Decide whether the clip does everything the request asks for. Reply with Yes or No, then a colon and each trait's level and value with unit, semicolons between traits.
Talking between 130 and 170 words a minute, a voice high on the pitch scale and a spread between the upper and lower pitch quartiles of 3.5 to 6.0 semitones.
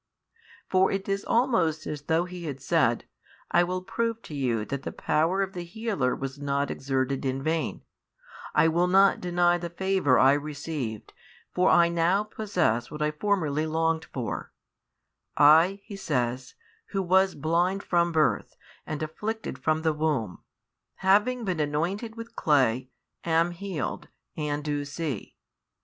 No: average, 150 wpm; medium, 160 Hz; average, 4.7 semitones